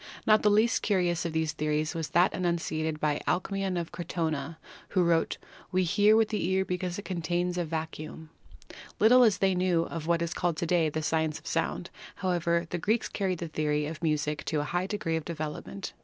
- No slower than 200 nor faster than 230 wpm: Yes, fast, 205 wpm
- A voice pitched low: No, medium, 170 Hz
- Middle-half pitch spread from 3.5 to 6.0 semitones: No, average, 2.7 semitones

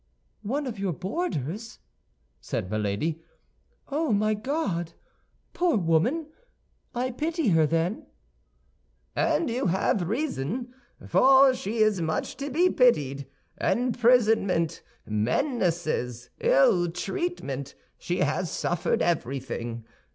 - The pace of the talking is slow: Yes, slow, 100 wpm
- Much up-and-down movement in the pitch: Yes, wide, 8.3 semitones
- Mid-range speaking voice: No, high, 195 Hz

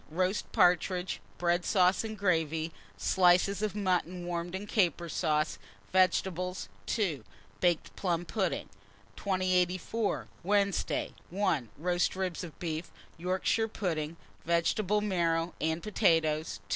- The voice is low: No, medium, 180 Hz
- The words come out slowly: Yes, slow, 110 wpm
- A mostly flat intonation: Yes, narrow, 2.3 semitones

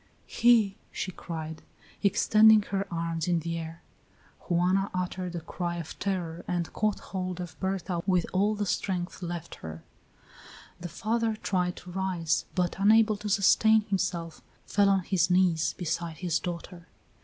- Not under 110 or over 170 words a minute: Yes, average, 150 wpm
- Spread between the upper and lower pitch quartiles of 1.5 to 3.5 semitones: Yes, average, 2.7 semitones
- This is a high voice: No, medium, 180 Hz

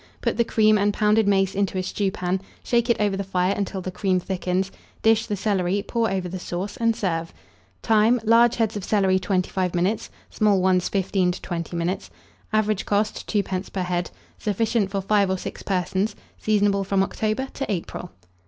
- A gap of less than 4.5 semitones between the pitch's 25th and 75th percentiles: Yes, narrow, 2.5 semitones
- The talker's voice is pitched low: No, high, 195 Hz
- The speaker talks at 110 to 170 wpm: No, average, 180 wpm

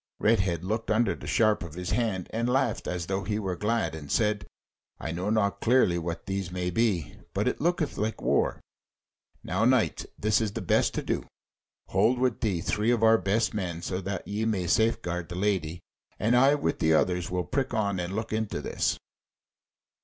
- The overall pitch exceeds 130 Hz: No, low, 100 Hz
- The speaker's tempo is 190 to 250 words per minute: Yes, average, 195 wpm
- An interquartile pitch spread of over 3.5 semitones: Yes, average, 4.0 semitones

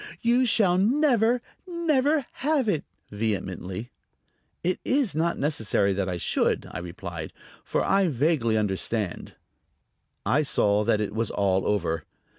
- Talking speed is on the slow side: Yes, slow, 130 wpm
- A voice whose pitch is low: Yes, low, 125 Hz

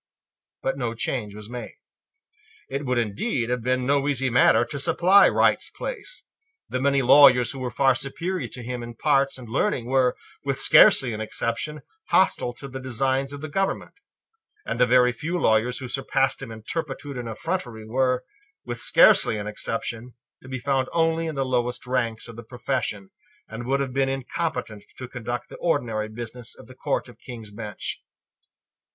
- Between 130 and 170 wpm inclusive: No, average, 180 wpm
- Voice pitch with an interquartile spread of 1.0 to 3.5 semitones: Yes, average, 2.7 semitones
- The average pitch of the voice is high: No, low, 125 Hz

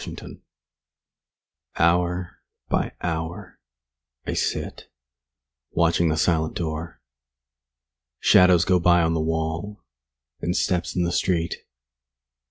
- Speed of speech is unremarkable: No, slow, 100 wpm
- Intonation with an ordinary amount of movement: No, narrow, 1.5 semitones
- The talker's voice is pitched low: Yes, very low, 85 Hz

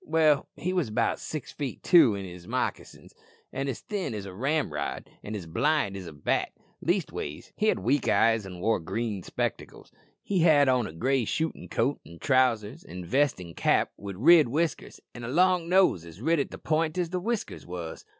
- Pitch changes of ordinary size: No, wide, 8.6 semitones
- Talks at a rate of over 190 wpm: Yes, average, 200 wpm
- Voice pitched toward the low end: Yes, low, 125 Hz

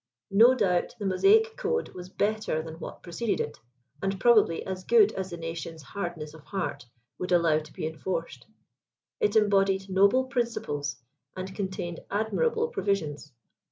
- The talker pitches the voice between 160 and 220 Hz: Yes, high, 190 Hz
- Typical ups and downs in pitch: Yes, average, 4.9 semitones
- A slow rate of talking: No, average, 160 wpm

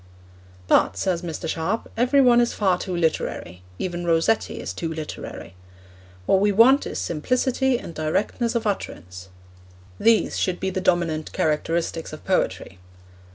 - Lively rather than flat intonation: Yes, wide, 5.8 semitones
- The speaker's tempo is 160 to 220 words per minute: No, average, 145 wpm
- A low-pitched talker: No, medium, 180 Hz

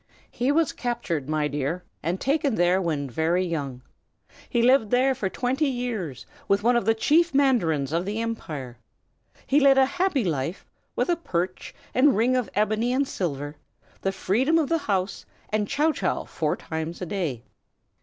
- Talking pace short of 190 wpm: Yes, average, 175 wpm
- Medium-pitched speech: No, high, 210 Hz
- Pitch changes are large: Yes, wide, 8.0 semitones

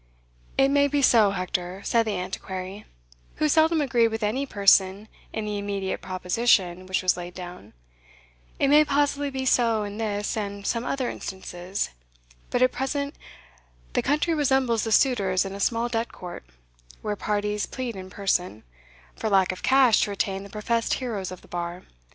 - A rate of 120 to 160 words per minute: No, average, 170 wpm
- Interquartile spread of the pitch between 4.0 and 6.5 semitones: Yes, average, 5.1 semitones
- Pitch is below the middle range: No, high, 210 Hz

